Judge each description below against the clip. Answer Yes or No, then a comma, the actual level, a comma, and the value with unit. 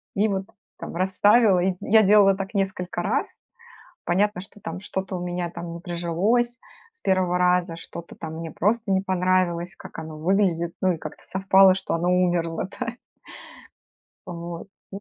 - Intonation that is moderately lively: No, narrow, 2.2 semitones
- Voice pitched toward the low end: No, medium, 185 Hz